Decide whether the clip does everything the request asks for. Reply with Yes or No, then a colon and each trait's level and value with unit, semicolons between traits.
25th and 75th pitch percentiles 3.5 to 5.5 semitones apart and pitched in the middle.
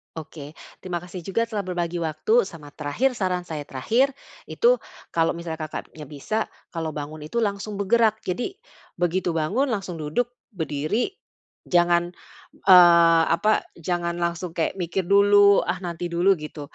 Yes: average, 3.9 semitones; medium, 175 Hz